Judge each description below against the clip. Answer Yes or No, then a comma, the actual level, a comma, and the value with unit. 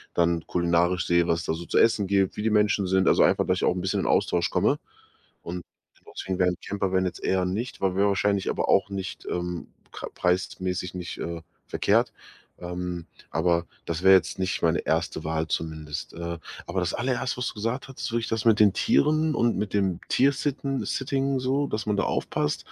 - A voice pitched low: Yes, very low, 95 Hz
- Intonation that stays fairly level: No, average, 4.0 semitones